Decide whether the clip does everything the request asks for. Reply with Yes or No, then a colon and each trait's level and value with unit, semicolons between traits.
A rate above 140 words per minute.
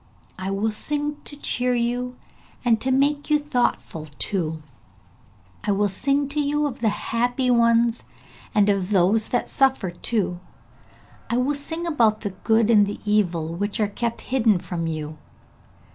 Yes: average, 160 wpm